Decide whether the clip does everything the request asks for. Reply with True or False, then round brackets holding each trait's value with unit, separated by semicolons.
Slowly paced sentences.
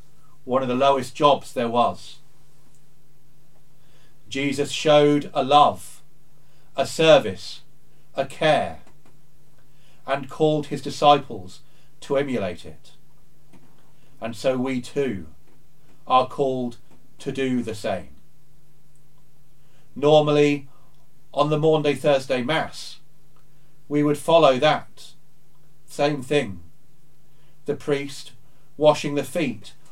True (100 wpm)